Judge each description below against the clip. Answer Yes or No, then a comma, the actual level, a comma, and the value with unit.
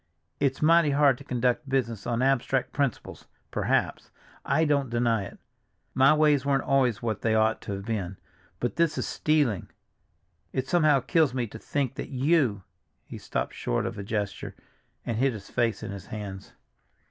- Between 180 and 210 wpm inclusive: No, average, 165 wpm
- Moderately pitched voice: No, low, 125 Hz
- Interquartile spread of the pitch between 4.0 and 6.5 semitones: Yes, average, 4.3 semitones